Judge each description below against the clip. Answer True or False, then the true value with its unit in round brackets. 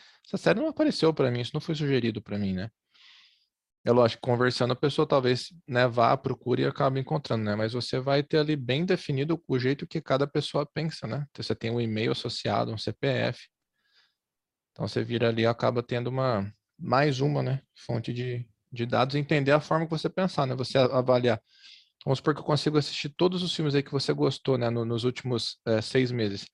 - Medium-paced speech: False (205 wpm)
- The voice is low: True (130 Hz)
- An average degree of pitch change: True (3.8 semitones)